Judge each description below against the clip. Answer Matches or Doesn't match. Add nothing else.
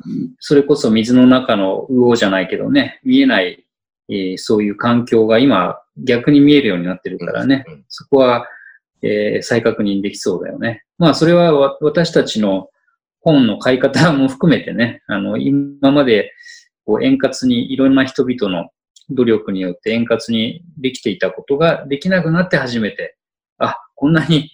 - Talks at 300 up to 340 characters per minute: Matches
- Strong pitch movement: Matches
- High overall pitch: Doesn't match